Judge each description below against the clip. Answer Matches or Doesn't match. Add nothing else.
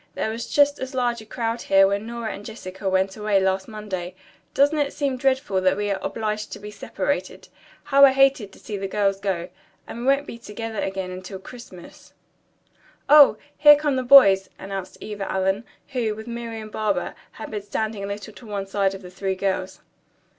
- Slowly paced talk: Doesn't match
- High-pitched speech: Matches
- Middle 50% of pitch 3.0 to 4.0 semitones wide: Matches